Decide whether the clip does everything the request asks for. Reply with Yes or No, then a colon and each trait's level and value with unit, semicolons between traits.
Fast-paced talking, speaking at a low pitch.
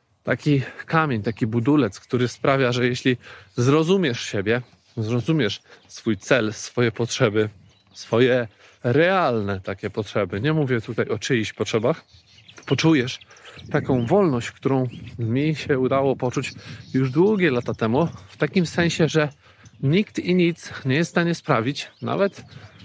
No: average, 130 wpm; low, 125 Hz